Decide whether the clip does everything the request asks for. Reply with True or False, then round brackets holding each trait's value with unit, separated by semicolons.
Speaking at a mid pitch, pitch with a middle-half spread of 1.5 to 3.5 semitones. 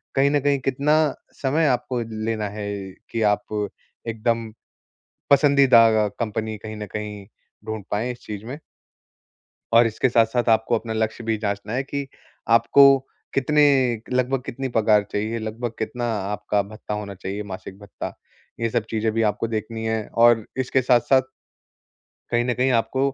False (115 Hz; 2.8 semitones)